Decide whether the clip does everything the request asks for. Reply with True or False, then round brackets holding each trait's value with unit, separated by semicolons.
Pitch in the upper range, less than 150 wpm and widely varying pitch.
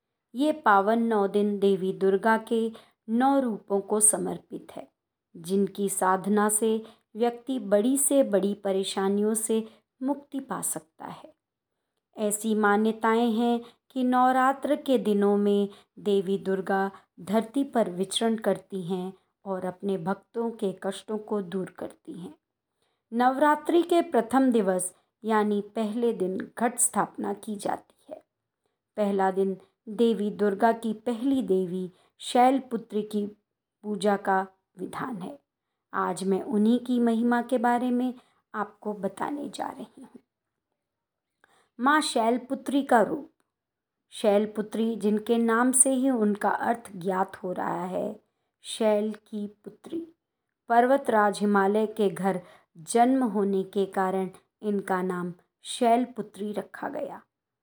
False (215 Hz; 125 wpm; 3.3 semitones)